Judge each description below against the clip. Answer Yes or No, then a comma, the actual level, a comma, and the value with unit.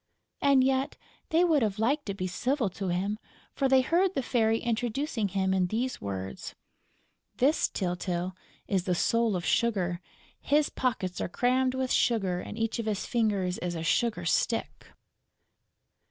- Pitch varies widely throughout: Yes, wide, 5.9 semitones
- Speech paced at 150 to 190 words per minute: Yes, average, 160 wpm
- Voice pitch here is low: No, high, 220 Hz